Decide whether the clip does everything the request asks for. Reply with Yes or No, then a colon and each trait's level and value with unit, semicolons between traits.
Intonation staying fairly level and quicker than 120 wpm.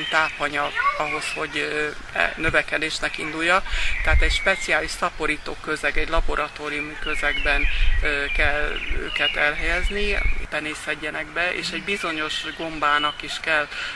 No: narrow, 2.1 semitones; slow, 105 wpm